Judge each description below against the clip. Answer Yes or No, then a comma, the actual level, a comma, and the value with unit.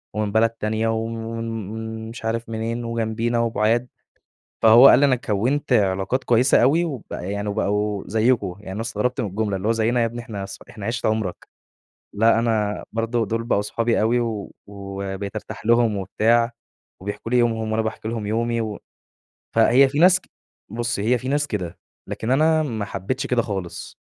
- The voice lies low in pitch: Yes, low, 115 Hz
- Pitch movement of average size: No, narrow, 2.2 semitones